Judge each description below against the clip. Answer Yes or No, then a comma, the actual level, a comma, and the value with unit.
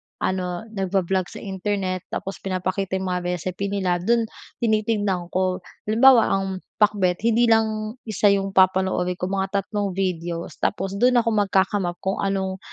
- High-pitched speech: Yes, high, 195 Hz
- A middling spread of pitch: No, narrow, 2.1 semitones